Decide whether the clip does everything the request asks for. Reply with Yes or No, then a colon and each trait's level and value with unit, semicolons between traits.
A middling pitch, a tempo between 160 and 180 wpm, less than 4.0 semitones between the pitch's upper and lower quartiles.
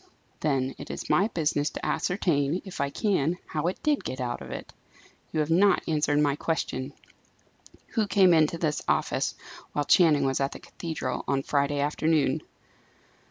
Yes: medium, 150 Hz; average, 165 wpm; average, 3.5 semitones